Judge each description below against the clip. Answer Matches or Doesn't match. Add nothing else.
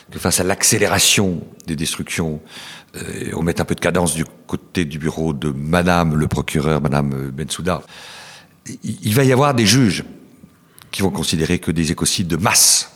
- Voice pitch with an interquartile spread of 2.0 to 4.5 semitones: Matches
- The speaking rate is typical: Matches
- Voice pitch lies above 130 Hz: Doesn't match